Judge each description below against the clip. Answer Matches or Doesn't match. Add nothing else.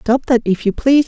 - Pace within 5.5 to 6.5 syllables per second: Matches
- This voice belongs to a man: Doesn't match